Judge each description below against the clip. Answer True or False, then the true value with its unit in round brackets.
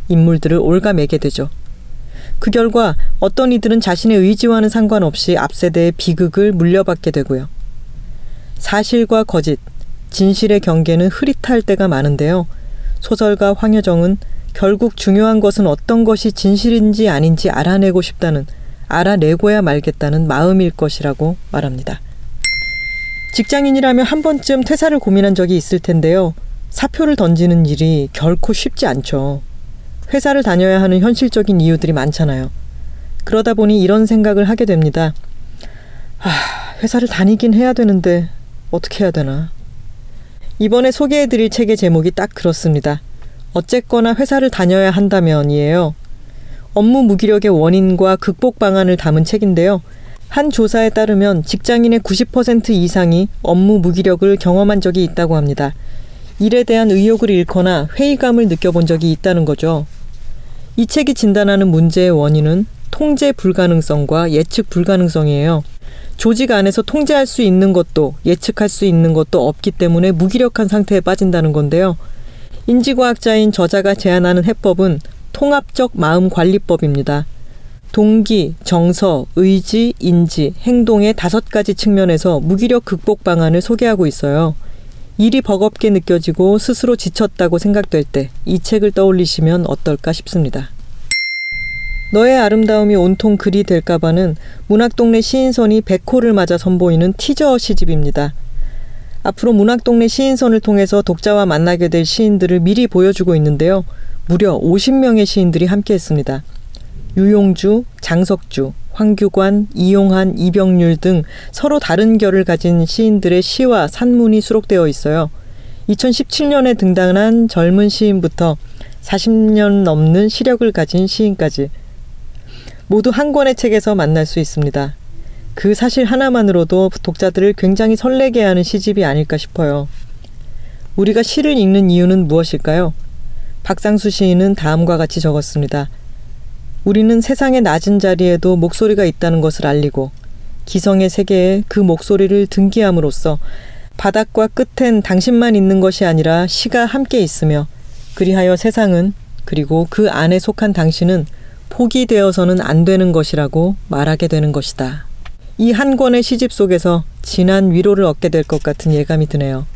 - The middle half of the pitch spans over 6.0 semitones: False (5.2 semitones)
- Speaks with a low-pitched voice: False (190 Hz)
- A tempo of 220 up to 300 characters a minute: False (315 characters per minute)